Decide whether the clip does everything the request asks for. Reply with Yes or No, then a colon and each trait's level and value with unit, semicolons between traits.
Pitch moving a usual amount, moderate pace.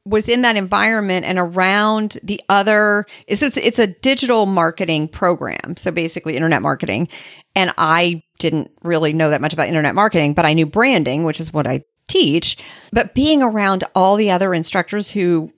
Yes: average, 4.6 semitones; average, 175 wpm